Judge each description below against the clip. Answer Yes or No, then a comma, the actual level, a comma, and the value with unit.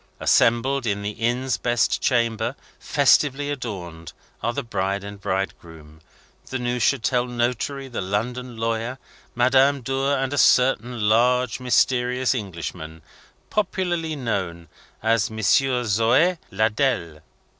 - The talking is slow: Yes, slow, 115 wpm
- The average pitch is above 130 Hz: No, low, 120 Hz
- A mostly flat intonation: No, average, 4.1 semitones